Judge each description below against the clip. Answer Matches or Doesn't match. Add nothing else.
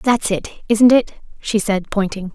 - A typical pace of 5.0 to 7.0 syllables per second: Doesn't match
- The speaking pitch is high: Matches